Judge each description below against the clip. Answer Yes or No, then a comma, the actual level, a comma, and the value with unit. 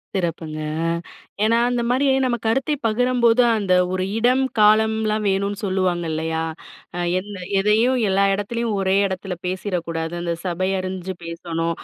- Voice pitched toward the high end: Yes, high, 195 Hz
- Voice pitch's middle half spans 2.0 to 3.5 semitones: No, average, 4.1 semitones